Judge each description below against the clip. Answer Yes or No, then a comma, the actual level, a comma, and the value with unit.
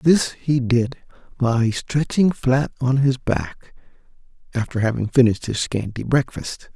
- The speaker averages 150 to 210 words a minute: No, slow, 135 wpm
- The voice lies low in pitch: Yes, low, 125 Hz